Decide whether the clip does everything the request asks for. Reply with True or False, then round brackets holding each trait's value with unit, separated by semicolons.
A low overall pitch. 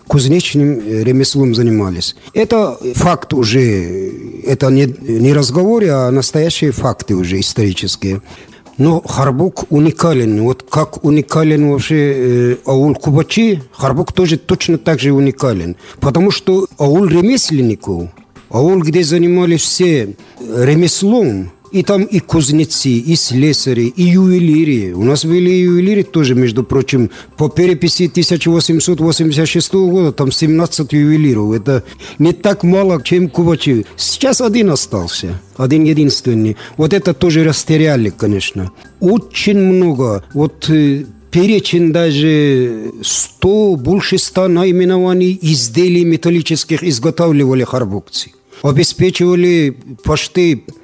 False (155 Hz)